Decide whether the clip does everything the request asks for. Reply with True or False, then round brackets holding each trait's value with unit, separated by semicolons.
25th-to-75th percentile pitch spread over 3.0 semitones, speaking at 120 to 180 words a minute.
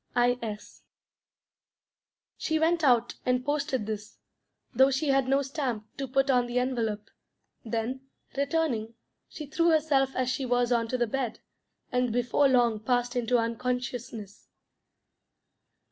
False (2.6 semitones; 135 wpm)